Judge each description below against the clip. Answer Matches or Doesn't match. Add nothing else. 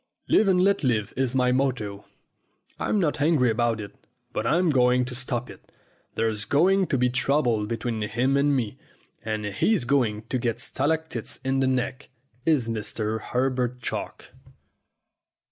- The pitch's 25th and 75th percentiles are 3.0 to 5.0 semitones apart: Matches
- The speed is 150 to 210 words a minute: Matches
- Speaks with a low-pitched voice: Matches